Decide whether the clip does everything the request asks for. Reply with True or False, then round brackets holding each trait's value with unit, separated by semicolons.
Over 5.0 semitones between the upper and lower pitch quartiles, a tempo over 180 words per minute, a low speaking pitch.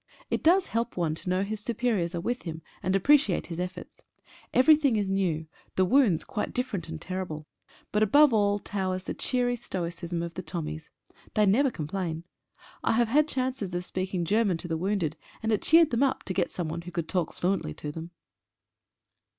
False (5.5 semitones; 190 wpm; 190 Hz)